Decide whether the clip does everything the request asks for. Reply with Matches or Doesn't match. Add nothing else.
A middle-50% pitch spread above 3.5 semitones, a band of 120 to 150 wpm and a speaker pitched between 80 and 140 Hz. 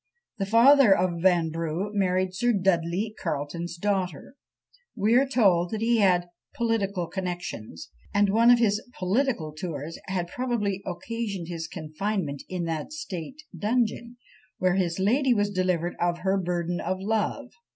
Doesn't match